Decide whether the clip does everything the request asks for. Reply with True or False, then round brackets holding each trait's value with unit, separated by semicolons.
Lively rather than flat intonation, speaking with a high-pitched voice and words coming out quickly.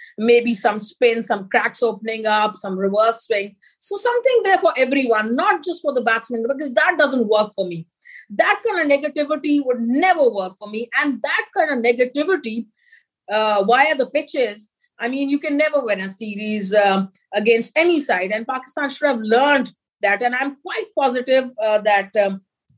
False (5.7 semitones; 245 Hz; 180 wpm)